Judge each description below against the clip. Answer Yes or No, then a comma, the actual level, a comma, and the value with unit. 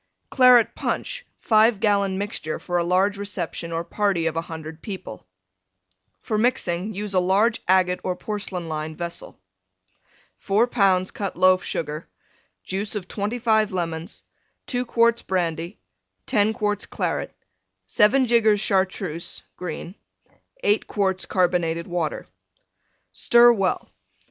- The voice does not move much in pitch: No, average, 3.8 semitones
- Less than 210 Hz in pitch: Yes, high, 190 Hz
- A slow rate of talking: Yes, slow, 120 wpm